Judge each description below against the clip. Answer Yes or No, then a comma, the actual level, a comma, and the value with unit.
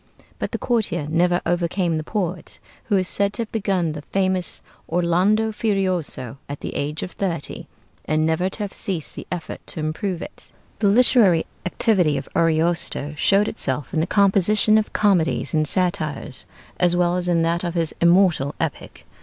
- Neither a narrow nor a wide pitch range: Yes, average, 3.5 semitones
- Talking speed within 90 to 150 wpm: No, average, 170 wpm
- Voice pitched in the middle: Yes, medium, 175 Hz